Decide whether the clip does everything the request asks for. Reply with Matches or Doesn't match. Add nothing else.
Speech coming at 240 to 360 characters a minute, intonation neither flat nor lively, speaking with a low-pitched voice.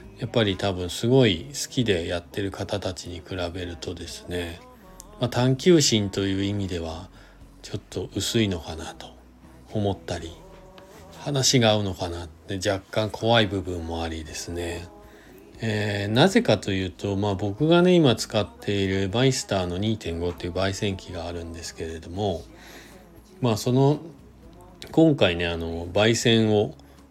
Matches